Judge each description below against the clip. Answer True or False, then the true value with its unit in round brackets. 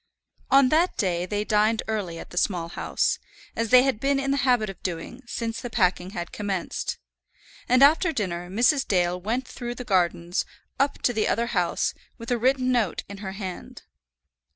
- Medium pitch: False (220 Hz)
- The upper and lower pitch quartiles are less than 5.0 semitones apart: False (5.4 semitones)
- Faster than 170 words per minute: True (185 wpm)